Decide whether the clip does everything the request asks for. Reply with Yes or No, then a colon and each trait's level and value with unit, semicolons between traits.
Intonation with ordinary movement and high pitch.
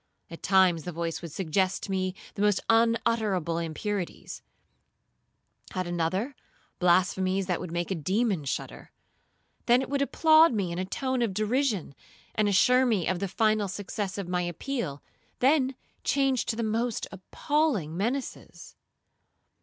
Yes: average, 4.9 semitones; high, 195 Hz